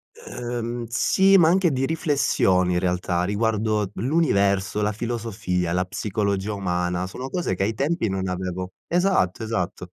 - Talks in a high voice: No, low, 105 Hz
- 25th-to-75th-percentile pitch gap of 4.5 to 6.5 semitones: Yes, average, 5.0 semitones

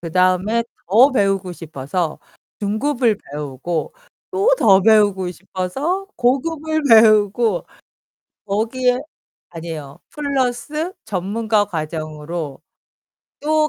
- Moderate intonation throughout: No, wide, 6.5 semitones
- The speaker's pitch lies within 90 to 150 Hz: No, high, 205 Hz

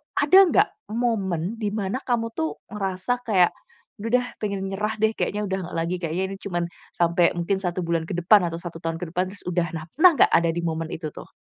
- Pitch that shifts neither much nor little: Yes, average, 4.2 semitones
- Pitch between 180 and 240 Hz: Yes, high, 190 Hz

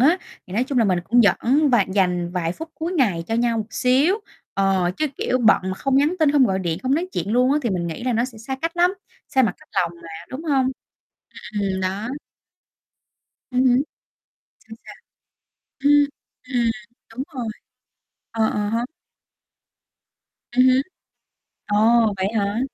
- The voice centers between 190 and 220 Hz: No, high, 235 Hz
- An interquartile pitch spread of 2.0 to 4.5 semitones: No, average, 5.2 semitones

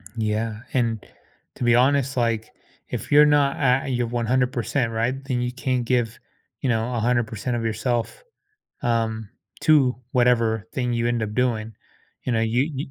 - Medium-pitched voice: No, low, 120 Hz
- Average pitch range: No, narrow, 2.1 semitones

